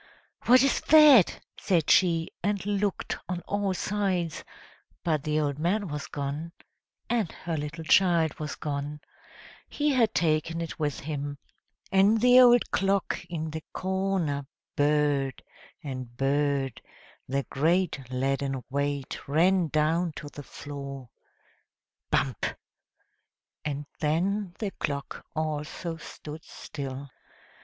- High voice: No, medium, 155 Hz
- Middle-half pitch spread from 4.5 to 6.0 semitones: Yes, average, 4.9 semitones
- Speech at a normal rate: No, slow, 120 wpm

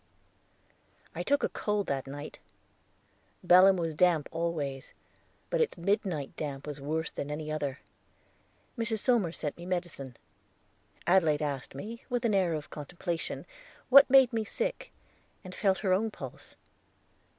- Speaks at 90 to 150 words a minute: Yes, average, 140 wpm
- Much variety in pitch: Yes, wide, 5.8 semitones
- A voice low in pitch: No, medium, 175 Hz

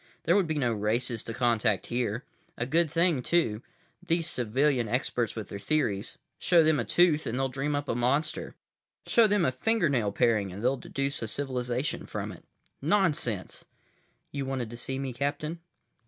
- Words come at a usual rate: Yes, average, 170 wpm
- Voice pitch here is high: No, low, 130 Hz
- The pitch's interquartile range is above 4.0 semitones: Yes, average, 4.7 semitones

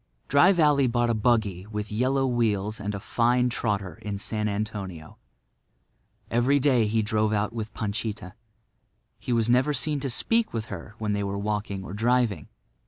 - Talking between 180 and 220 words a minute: No, average, 170 wpm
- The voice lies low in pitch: Yes, low, 110 Hz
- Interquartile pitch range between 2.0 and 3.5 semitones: Yes, average, 3.2 semitones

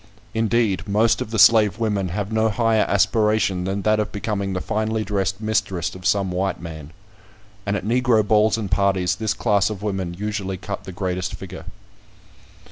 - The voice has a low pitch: Yes, low, 100 Hz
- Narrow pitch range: Yes, narrow, 2.3 semitones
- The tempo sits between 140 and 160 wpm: No, average, 175 wpm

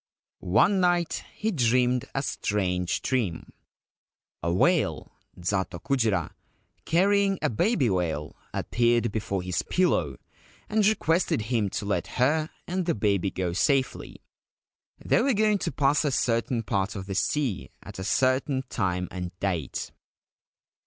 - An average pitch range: No, wide, 8.1 semitones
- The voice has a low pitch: Yes, low, 115 Hz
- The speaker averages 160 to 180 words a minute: No, average, 140 wpm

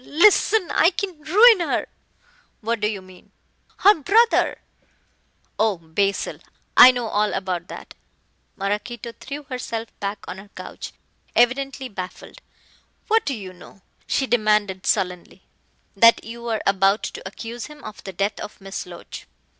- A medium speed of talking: Yes, average, 150 wpm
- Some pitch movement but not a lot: No, wide, 6.0 semitones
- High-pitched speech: Yes, high, 225 Hz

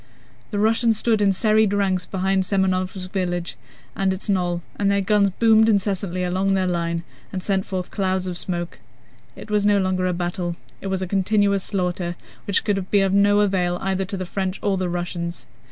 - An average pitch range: No, narrow, 1.7 semitones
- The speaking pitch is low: No, high, 190 Hz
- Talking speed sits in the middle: Yes, average, 190 wpm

